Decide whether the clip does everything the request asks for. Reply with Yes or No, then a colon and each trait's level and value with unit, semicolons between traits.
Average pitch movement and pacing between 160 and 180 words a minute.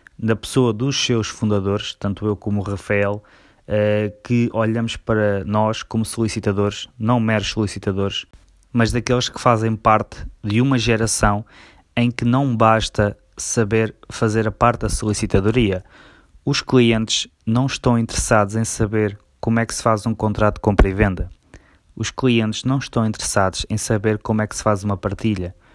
No: narrow, 2.1 semitones; average, 165 wpm